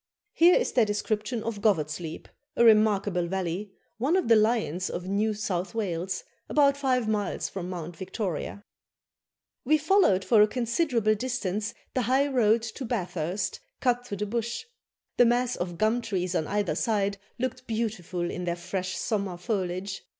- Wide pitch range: No, average, 4.3 semitones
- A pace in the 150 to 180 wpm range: Yes, average, 160 wpm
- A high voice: Yes, high, 210 Hz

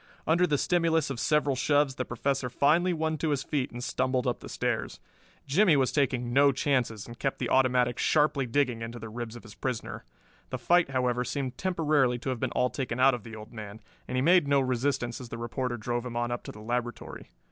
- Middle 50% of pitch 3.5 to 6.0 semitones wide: No, average, 3.1 semitones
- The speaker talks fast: Yes, fast, 225 wpm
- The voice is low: Yes, low, 130 Hz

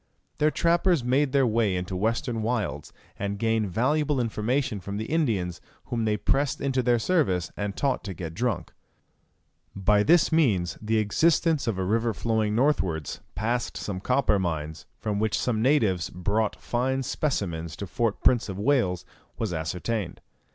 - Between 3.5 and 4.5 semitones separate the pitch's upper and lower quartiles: No, average, 5.0 semitones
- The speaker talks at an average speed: Yes, average, 165 wpm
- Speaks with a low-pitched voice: Yes, low, 110 Hz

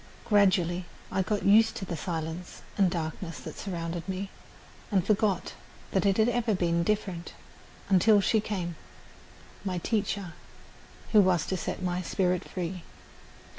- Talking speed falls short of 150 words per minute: Yes, average, 140 wpm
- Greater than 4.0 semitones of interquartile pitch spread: No, average, 2.7 semitones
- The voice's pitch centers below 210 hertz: Yes, medium, 185 Hz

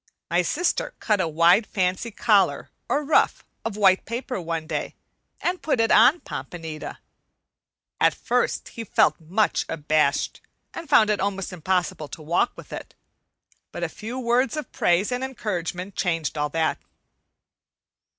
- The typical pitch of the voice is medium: No, high, 195 Hz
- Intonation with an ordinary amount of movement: No, wide, 5.9 semitones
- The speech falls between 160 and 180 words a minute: No, average, 150 wpm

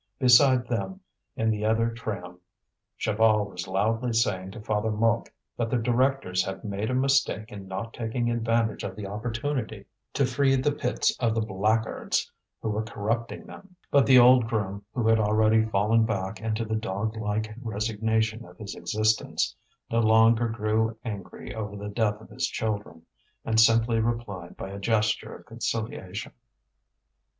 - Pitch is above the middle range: No, low, 110 Hz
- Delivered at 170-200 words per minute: No, average, 160 wpm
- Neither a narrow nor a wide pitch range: No, narrow, 1.9 semitones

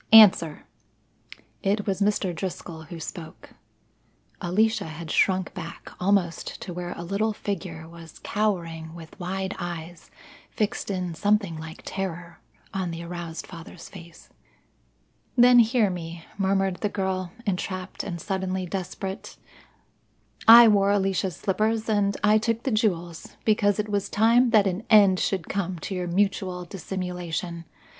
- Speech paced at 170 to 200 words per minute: No, slow, 135 wpm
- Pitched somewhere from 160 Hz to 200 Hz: Yes, high, 190 Hz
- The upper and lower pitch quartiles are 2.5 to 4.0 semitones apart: Yes, average, 3.1 semitones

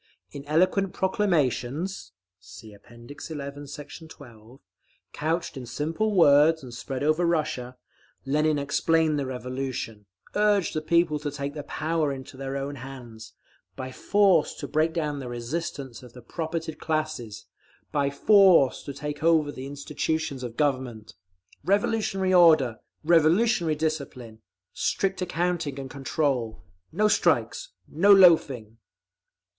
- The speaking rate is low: Yes, slow, 130 wpm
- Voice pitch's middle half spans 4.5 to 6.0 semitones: No, average, 4.1 semitones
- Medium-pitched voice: Yes, medium, 150 Hz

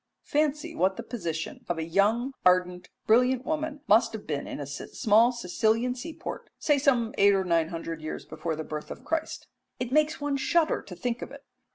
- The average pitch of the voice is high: Yes, high, 225 Hz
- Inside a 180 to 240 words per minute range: Yes, average, 200 wpm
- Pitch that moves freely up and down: Yes, wide, 7.7 semitones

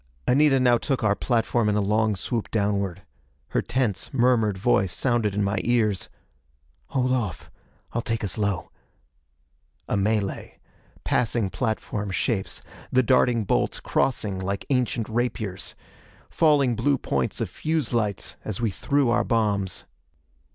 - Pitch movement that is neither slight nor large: Yes, average, 3.7 semitones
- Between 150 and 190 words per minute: No, slow, 135 wpm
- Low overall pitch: Yes, low, 110 Hz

